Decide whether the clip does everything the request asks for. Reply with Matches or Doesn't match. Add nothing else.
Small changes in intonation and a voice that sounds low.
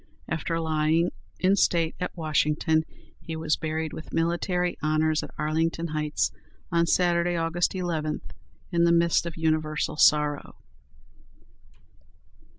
Doesn't match